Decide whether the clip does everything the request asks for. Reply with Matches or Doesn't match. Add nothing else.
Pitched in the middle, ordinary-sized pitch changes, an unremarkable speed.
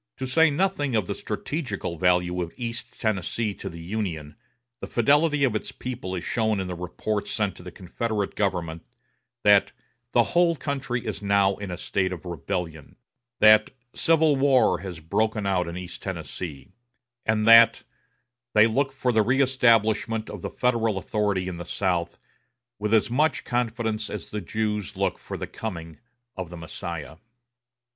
Doesn't match